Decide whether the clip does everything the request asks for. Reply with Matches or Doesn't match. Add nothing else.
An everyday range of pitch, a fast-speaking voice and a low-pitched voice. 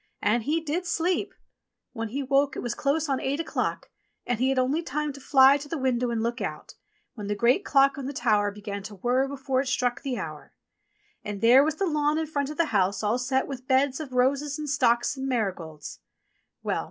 Doesn't match